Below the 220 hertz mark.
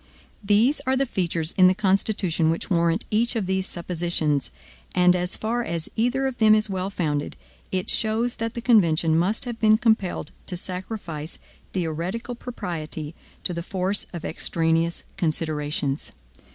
Yes: medium, 185 Hz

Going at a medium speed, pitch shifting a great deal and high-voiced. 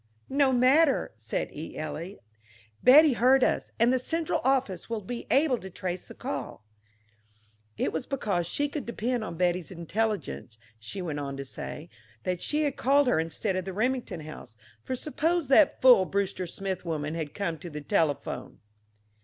Yes: average, 170 wpm; wide, 7.7 semitones; high, 200 Hz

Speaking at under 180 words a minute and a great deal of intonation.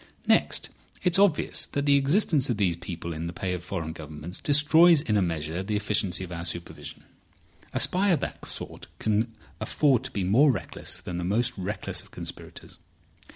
No: average, 185 wpm; wide, 8.5 semitones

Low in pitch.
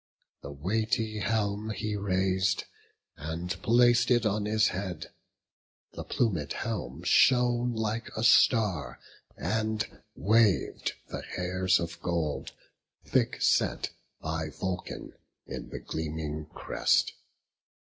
Yes: low, 100 Hz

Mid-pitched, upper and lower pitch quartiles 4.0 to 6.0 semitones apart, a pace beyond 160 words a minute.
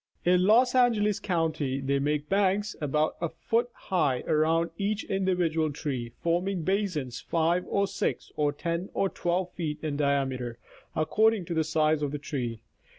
No: medium, 165 Hz; average, 4.6 semitones; average, 155 wpm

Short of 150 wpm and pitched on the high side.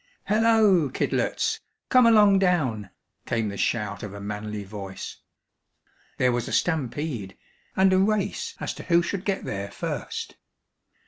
No: average, 140 wpm; medium, 145 Hz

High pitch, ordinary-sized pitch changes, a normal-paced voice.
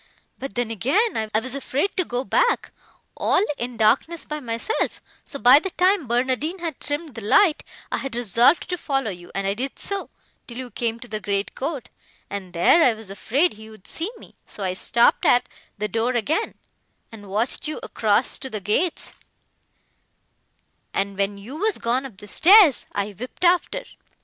No: high, 245 Hz; wide, 6.3 semitones; average, 185 wpm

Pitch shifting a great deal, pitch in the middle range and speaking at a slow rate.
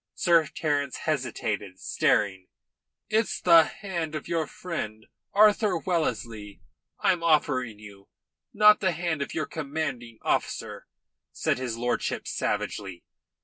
Yes: wide, 7.2 semitones; medium, 155 Hz; slow, 115 wpm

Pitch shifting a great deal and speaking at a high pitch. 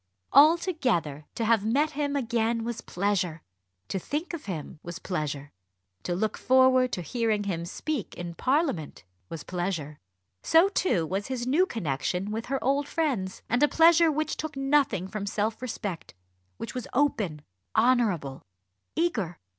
Yes: wide, 7.7 semitones; high, 225 Hz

